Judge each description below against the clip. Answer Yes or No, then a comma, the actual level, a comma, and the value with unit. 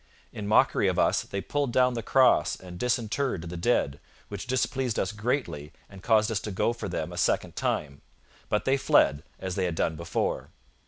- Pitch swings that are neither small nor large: No, wide, 5.9 semitones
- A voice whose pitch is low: Yes, low, 105 Hz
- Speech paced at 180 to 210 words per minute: Yes, average, 195 wpm